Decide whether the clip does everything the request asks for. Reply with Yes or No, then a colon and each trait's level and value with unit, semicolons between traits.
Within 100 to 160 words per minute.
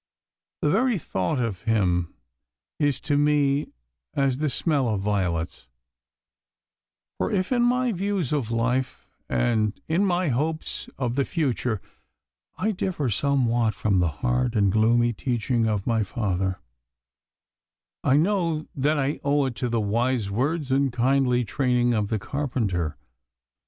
Yes: average, 140 wpm